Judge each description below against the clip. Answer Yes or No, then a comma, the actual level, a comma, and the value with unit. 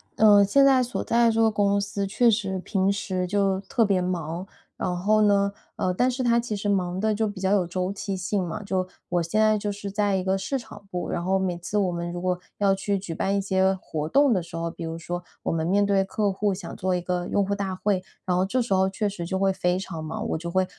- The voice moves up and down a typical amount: No, narrow, 2.1 semitones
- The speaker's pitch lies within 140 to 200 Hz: Yes, high, 195 Hz